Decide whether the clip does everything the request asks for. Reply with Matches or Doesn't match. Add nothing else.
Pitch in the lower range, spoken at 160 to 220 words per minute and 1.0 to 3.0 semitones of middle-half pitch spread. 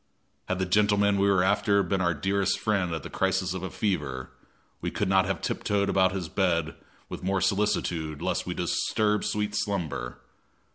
Matches